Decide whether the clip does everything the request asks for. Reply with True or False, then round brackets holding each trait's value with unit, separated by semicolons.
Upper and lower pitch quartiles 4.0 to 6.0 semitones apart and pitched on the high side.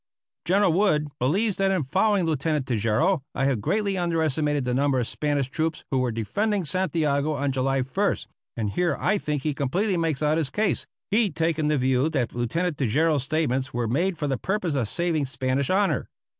False (5.0 semitones; 150 Hz)